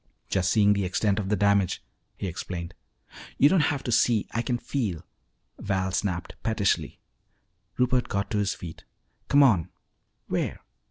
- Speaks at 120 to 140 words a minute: No, average, 155 wpm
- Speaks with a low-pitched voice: Yes, low, 100 Hz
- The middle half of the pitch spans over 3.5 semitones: Yes, average, 4.0 semitones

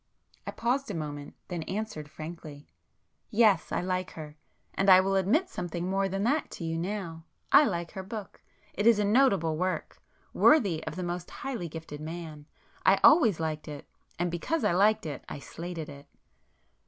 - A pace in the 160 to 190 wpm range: Yes, average, 170 wpm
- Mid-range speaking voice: Yes, medium, 180 Hz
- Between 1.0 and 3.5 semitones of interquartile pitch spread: No, average, 4.3 semitones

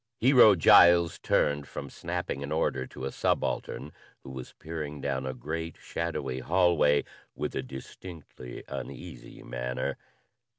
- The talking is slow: Yes, slow, 130 wpm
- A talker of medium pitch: No, very low, 75 Hz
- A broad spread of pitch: No, average, 4.0 semitones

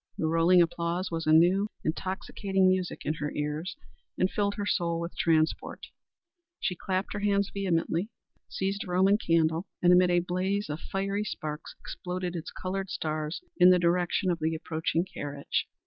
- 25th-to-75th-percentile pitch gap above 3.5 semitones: No, average, 2.8 semitones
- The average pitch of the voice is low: No, medium, 180 Hz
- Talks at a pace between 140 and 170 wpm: Yes, average, 165 wpm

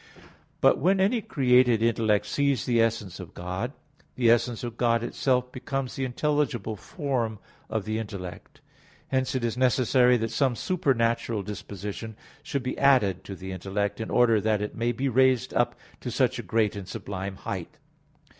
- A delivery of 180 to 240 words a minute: No, average, 165 wpm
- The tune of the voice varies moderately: Yes, average, 3.7 semitones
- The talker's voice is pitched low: Yes, low, 115 Hz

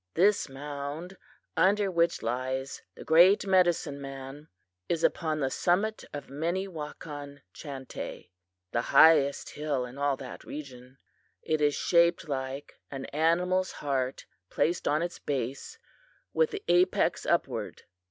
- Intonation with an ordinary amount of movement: Yes, average, 4.1 semitones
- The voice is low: No, medium, 150 Hz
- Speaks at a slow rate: Yes, slow, 125 wpm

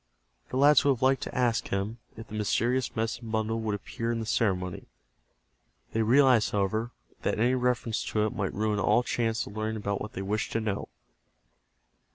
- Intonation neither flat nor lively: No, narrow, 2.3 semitones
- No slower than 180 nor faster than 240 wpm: Yes, average, 185 wpm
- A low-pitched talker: Yes, low, 110 Hz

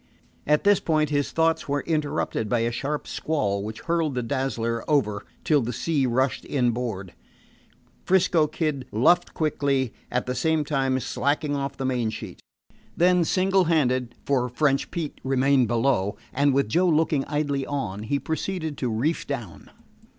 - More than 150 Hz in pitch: No, medium, 140 Hz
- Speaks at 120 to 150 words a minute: No, average, 160 wpm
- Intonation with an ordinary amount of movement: Yes, average, 4.0 semitones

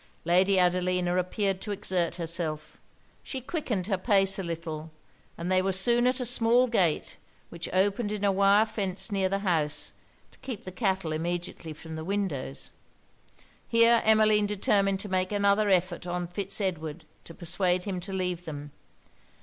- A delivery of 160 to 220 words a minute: Yes, average, 165 wpm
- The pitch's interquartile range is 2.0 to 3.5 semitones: Yes, average, 2.8 semitones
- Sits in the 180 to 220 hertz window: Yes, high, 190 Hz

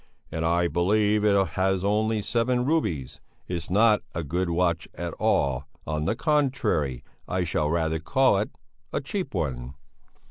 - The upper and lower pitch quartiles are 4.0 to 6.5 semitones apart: Yes, average, 5.0 semitones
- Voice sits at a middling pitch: No, very low, 90 Hz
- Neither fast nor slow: Yes, average, 150 wpm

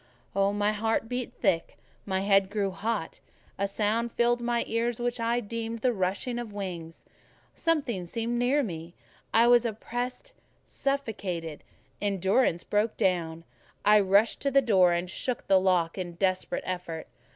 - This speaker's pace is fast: No, average, 150 wpm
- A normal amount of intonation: Yes, average, 4.2 semitones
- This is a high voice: Yes, high, 210 Hz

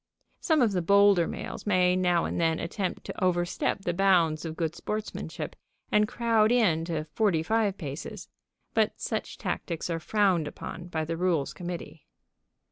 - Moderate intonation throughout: Yes, average, 3.6 semitones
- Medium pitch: Yes, medium, 180 Hz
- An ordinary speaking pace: Yes, average, 160 wpm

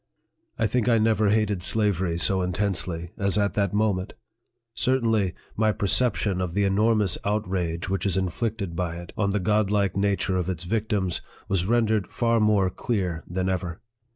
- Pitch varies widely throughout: No, average, 2.8 semitones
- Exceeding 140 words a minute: Yes, average, 165 wpm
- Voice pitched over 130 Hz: No, low, 100 Hz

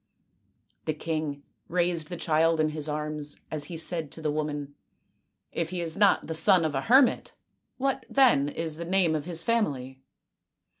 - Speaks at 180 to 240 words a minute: Yes, average, 185 wpm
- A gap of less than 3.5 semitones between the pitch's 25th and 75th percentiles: Yes, average, 2.7 semitones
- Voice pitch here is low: No, medium, 160 Hz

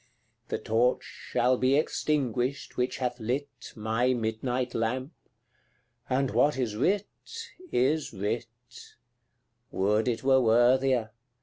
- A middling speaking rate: No, slow, 110 wpm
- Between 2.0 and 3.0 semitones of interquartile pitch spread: Yes, average, 2.7 semitones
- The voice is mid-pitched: No, low, 125 Hz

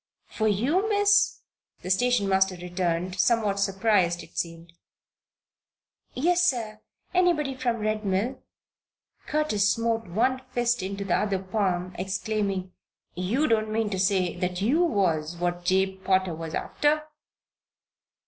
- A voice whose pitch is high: Yes, high, 200 Hz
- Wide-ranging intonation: No, average, 4.5 semitones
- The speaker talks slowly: Yes, slow, 130 wpm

